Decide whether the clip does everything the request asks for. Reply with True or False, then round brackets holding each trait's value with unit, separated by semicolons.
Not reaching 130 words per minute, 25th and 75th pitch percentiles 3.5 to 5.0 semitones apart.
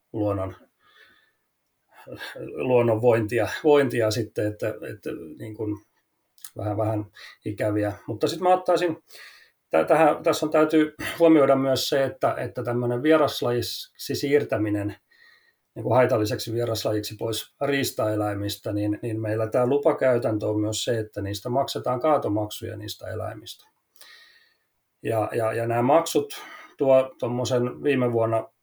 True (120 wpm; 4.4 semitones)